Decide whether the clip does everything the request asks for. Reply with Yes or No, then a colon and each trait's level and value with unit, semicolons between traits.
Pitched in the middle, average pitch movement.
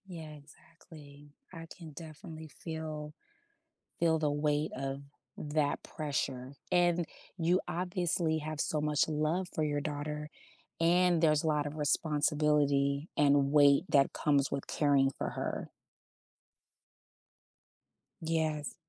No: medium, 150 Hz; narrow, 1.9 semitones